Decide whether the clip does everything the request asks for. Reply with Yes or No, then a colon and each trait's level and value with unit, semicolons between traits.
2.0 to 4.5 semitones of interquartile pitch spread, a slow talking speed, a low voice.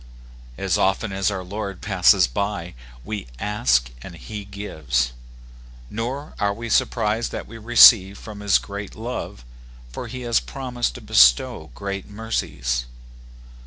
Yes: average, 3.6 semitones; slow, 130 wpm; low, 100 Hz